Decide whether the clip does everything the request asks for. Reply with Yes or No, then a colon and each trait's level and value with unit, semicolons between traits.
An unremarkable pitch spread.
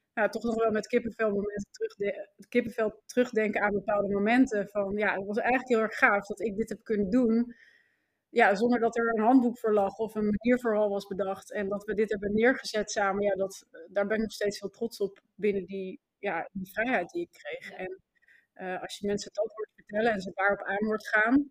No: narrow, 2.3 semitones